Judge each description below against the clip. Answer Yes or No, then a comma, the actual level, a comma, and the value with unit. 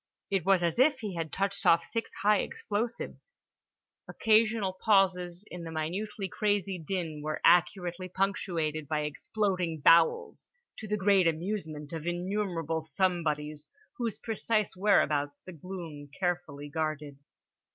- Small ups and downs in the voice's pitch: No, average, 4.0 semitones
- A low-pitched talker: No, medium, 180 Hz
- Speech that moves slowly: Yes, slow, 130 wpm